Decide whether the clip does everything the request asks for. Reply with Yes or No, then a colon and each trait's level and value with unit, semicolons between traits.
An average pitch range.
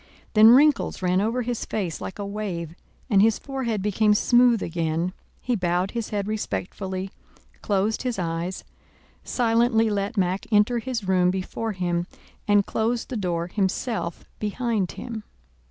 Yes: average, 3.8 semitones